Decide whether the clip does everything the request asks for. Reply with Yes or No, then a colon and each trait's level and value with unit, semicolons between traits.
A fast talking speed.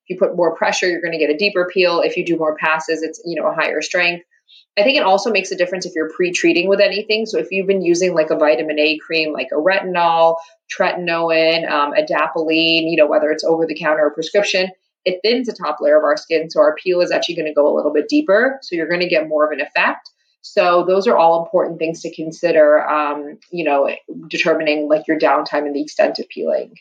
Yes: fast, 240 wpm